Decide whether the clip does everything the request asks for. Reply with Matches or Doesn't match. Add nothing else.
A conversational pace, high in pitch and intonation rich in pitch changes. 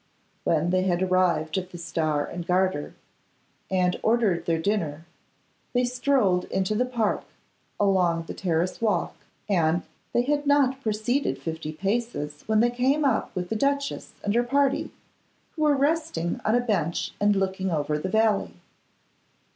Matches